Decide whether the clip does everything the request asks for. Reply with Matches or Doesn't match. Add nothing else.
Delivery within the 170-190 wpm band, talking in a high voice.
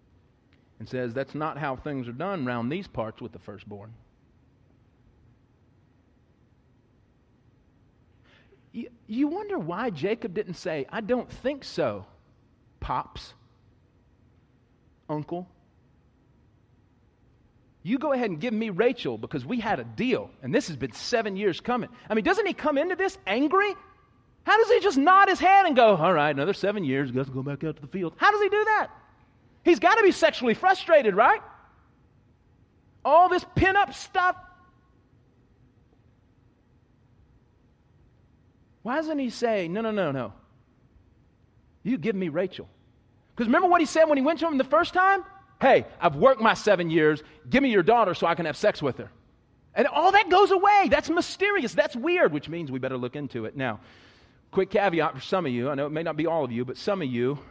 Matches